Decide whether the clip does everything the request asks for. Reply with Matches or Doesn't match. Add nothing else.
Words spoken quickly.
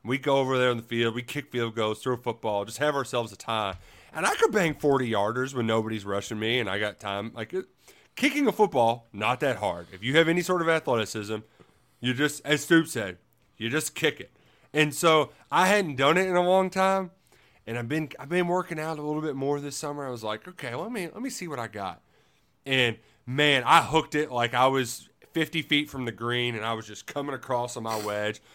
Matches